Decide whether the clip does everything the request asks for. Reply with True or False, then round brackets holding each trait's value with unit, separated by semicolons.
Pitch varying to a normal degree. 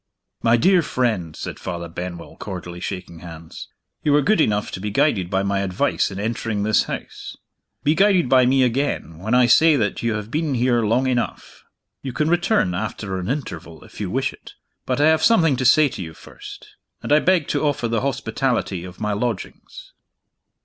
False (7.1 semitones)